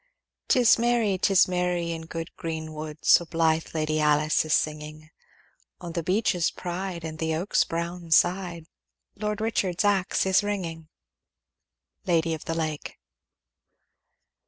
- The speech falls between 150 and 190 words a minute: No, slow, 135 wpm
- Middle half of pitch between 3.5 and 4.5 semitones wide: No, average, 2.8 semitones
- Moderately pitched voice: Yes, medium, 170 Hz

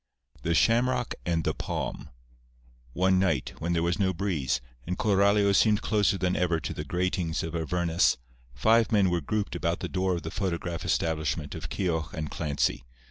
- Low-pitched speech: Yes, very low, 90 Hz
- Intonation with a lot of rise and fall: No, average, 3.2 semitones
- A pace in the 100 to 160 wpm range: No, average, 180 wpm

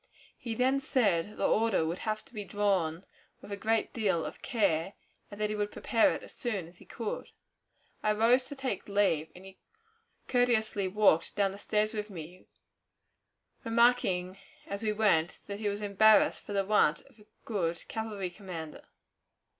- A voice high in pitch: Yes, high, 205 Hz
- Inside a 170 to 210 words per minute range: Yes, average, 175 wpm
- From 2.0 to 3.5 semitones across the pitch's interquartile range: Yes, average, 3.0 semitones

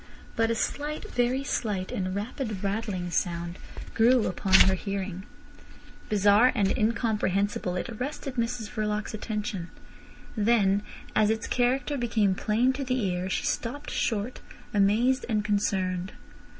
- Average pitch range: Yes, average, 3.7 semitones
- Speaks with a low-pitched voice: No, high, 215 Hz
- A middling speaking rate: No, slow, 130 wpm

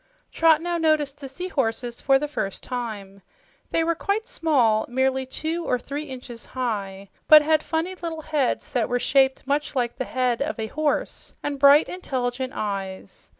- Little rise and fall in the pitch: No, average, 4.2 semitones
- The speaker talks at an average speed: Yes, average, 170 wpm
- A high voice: Yes, very high, 270 Hz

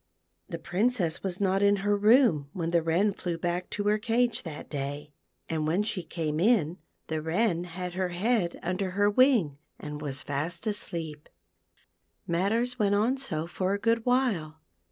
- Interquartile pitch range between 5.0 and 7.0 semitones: No, average, 4.4 semitones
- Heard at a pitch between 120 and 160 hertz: No, medium, 180 Hz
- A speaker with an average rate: Yes, average, 170 wpm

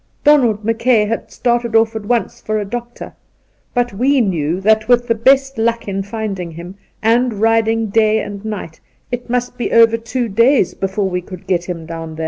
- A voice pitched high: Yes, high, 220 Hz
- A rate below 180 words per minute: No, average, 185 wpm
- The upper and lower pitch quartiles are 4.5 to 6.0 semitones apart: No, average, 3.4 semitones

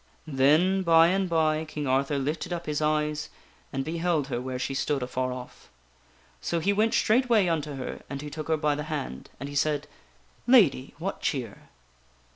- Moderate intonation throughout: Yes, average, 3.4 semitones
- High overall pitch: No, medium, 150 Hz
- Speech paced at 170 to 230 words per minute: Yes, average, 185 wpm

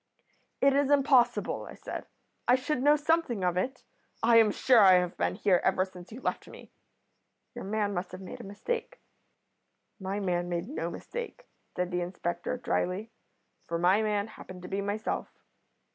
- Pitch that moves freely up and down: Yes, wide, 5.9 semitones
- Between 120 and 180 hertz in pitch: No, high, 205 Hz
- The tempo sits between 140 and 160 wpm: No, average, 175 wpm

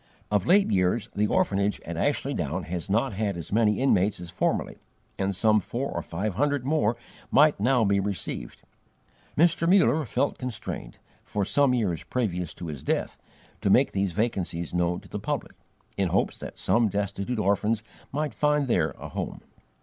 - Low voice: Yes, low, 105 Hz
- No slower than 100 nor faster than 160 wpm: No, average, 175 wpm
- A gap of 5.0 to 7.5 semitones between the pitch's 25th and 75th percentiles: Yes, average, 5.3 semitones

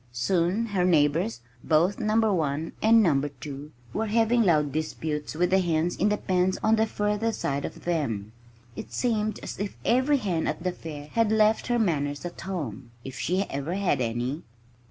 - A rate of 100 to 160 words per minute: No, average, 180 wpm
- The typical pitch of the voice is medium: Yes, medium, 175 Hz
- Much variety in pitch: Yes, wide, 6.3 semitones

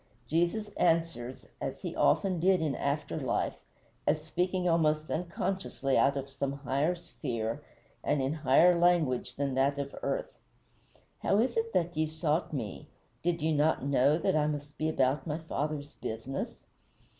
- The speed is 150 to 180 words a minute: Yes, average, 160 wpm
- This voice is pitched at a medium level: Yes, medium, 155 Hz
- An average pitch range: Yes, average, 3.7 semitones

